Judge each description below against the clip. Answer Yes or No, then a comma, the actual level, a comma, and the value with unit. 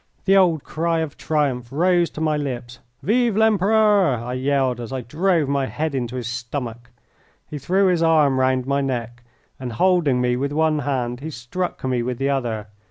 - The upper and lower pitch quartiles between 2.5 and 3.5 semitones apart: No, average, 5.0 semitones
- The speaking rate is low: No, average, 185 wpm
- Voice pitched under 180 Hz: Yes, medium, 140 Hz